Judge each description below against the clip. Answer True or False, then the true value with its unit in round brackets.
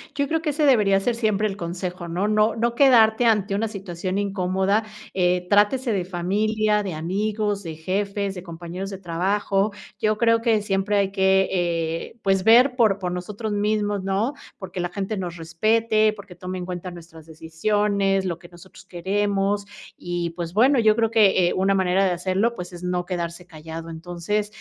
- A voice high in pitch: True (195 Hz)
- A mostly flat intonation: False (3.1 semitones)